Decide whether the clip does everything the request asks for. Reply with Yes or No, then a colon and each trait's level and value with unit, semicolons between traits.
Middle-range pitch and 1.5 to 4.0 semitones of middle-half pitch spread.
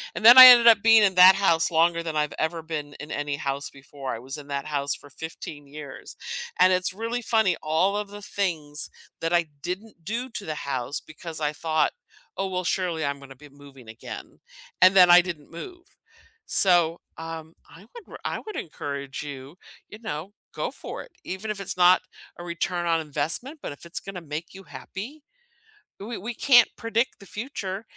No: medium, 170 Hz; average, 5.1 semitones